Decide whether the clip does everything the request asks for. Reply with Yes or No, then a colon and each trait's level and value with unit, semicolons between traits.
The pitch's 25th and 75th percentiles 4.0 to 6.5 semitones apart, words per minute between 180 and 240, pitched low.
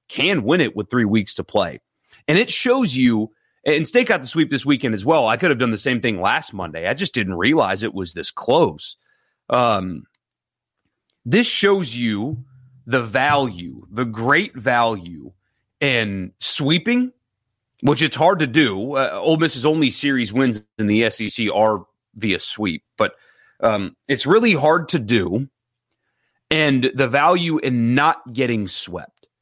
No: average, 5.3 semitones; average, 165 wpm; low, 130 Hz